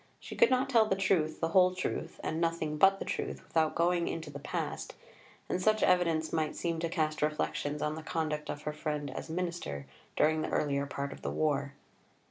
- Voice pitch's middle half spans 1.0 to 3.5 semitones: Yes, average, 2.8 semitones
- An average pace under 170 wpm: No, fast, 205 wpm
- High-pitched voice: No, medium, 160 Hz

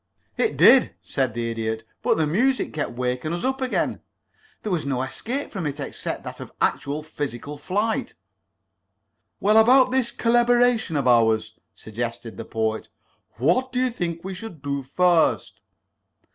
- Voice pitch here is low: No, medium, 160 Hz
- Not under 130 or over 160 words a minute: Yes, average, 155 wpm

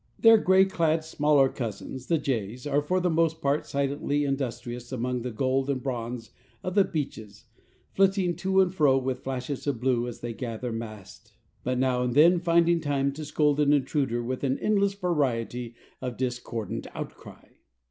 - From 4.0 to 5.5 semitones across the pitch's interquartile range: Yes, average, 4.6 semitones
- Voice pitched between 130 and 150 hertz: Yes, low, 135 Hz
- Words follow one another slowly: No, average, 170 wpm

